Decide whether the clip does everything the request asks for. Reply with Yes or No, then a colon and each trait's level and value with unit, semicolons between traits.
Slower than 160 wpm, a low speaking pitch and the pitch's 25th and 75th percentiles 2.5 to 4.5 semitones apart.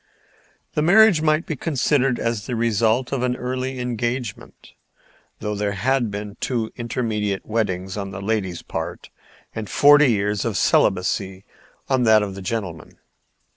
Yes: average, 145 wpm; low, 115 Hz; average, 4.0 semitones